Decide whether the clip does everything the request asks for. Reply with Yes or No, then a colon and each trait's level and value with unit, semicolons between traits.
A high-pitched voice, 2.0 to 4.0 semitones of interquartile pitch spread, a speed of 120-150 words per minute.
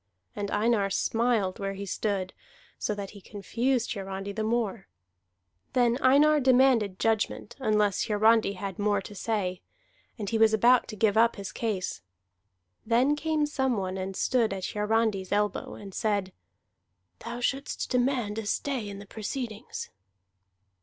Yes: high, 215 Hz; average, 3.2 semitones; average, 145 wpm